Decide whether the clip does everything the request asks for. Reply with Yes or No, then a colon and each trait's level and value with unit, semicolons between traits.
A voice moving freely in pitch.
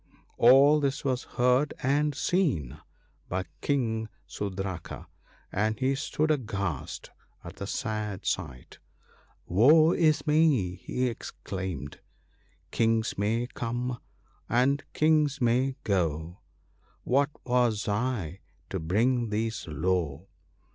Yes: wide, 6.0 semitones